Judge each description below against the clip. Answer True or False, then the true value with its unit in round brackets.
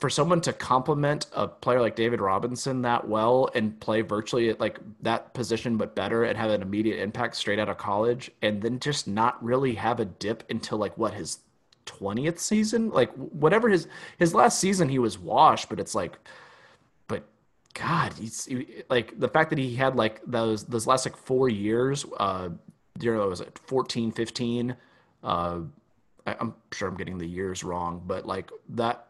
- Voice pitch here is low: True (120 Hz)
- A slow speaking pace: False (190 wpm)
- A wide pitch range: False (3.5 semitones)